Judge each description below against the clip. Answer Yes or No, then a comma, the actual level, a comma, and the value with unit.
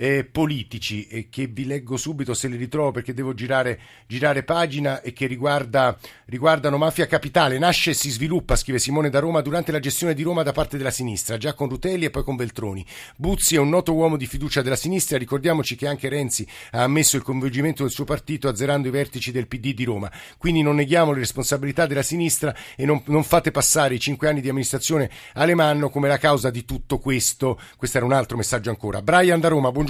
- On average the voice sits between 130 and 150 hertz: Yes, medium, 140 Hz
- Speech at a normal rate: No, fast, 210 wpm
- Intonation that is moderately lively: Yes, average, 3.1 semitones